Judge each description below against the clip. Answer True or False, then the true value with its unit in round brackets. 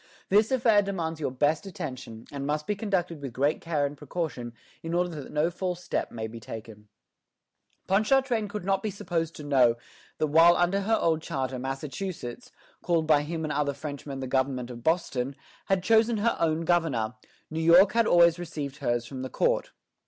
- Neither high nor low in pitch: True (160 Hz)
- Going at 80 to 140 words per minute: False (185 wpm)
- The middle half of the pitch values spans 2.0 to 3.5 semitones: False (5.2 semitones)